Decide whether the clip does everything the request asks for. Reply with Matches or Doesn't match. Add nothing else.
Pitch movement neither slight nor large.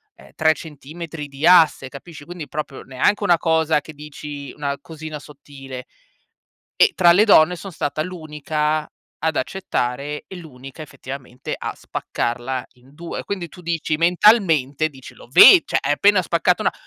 Matches